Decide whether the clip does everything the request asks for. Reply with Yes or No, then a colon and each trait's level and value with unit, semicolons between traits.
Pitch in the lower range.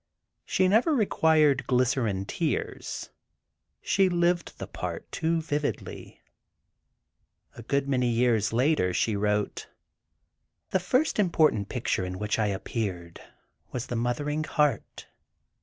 Yes: low, 130 Hz